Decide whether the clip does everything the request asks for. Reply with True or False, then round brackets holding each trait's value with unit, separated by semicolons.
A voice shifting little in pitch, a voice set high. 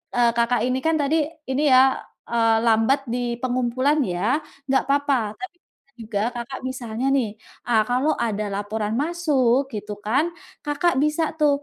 False (4.0 semitones; 255 Hz)